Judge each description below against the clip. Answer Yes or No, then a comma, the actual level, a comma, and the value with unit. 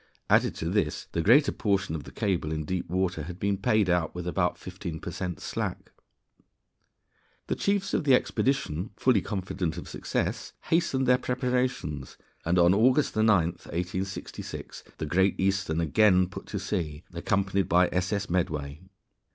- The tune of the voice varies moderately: Yes, average, 3.8 semitones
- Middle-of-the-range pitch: No, very low, 95 Hz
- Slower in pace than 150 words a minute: No, average, 155 wpm